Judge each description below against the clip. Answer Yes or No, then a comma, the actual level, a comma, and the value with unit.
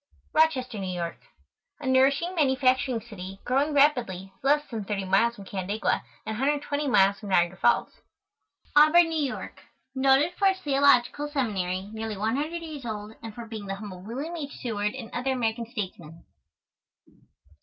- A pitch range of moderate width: No, wide, 5.8 semitones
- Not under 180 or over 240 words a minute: No, average, 160 wpm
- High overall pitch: Yes, high, 240 Hz